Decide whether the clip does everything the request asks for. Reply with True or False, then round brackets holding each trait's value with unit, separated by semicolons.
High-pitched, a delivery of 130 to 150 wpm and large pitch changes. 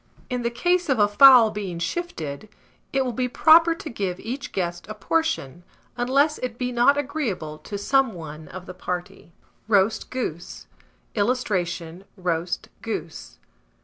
True (220 Hz; 145 wpm; 7.0 semitones)